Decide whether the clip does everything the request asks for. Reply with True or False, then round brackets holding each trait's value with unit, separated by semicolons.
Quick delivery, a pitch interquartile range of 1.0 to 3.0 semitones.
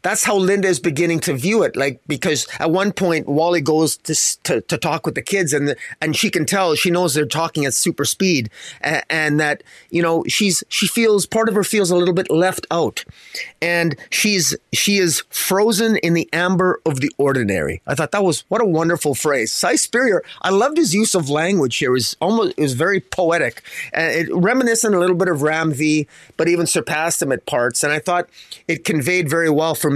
False (220 wpm; 3.6 semitones)